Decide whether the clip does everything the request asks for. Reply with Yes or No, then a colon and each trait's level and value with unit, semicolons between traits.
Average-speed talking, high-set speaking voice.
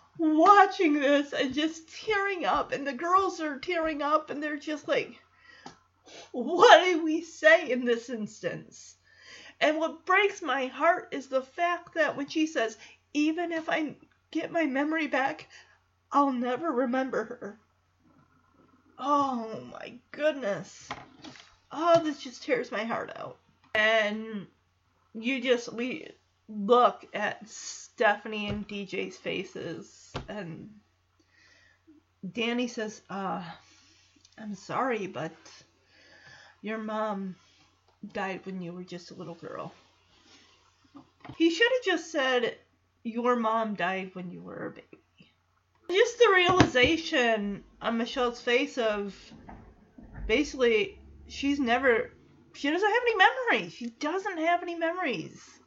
No: slow, 125 wpm; very high, 265 Hz